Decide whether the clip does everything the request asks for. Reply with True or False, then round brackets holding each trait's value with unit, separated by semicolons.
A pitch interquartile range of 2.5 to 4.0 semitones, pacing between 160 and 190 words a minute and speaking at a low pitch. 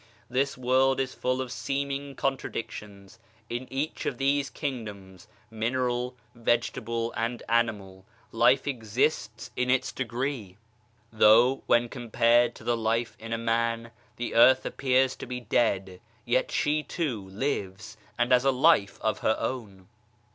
False (2.8 semitones; 140 wpm; 120 Hz)